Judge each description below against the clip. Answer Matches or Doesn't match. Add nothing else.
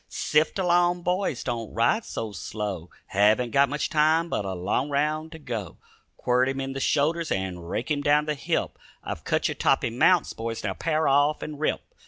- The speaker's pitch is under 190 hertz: Matches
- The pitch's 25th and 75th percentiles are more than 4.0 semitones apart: Matches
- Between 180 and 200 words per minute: Matches